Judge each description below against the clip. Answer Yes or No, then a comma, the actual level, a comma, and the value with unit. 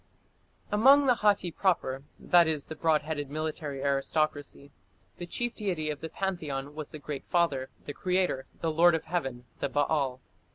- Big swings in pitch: No, average, 3.7 semitones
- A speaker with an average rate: Yes, average, 165 wpm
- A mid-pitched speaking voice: Yes, medium, 155 Hz